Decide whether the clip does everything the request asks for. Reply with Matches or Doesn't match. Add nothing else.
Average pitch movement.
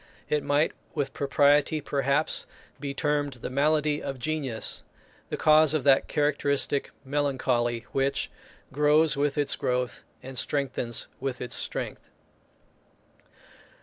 Doesn't match